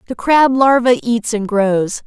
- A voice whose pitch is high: Yes, high, 235 Hz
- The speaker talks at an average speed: Yes, average, 175 wpm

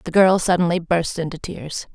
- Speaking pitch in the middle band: Yes, medium, 170 Hz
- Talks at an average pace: Yes, average, 185 wpm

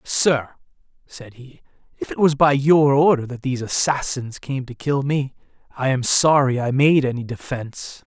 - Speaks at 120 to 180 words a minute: Yes, average, 170 wpm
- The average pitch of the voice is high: No, low, 135 Hz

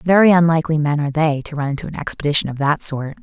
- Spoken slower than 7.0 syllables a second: No, 7.1 syllables/s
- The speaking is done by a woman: Yes, female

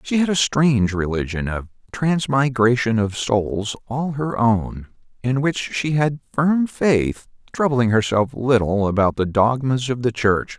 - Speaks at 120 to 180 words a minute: Yes, average, 155 wpm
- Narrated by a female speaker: No, male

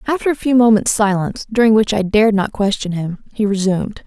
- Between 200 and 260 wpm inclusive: Yes, fast, 205 wpm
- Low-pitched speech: No, high, 210 Hz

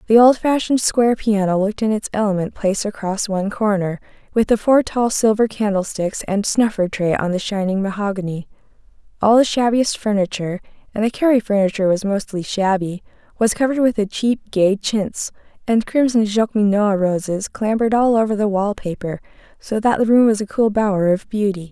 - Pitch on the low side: No, high, 210 Hz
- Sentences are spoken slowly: No, average, 175 wpm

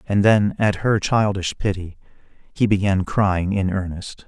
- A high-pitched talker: No, low, 100 Hz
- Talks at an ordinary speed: Yes, average, 155 wpm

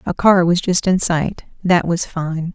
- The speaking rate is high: No, average, 190 wpm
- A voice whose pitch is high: No, medium, 175 Hz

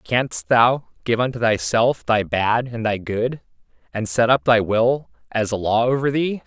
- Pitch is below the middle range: Yes, low, 120 Hz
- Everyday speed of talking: Yes, average, 185 wpm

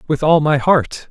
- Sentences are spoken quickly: Yes, fast, 215 wpm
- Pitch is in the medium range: Yes, medium, 150 Hz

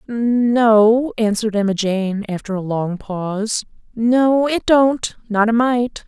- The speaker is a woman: Yes, female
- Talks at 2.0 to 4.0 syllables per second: Yes, 3.5 syllables/s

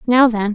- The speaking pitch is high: Yes, high, 230 Hz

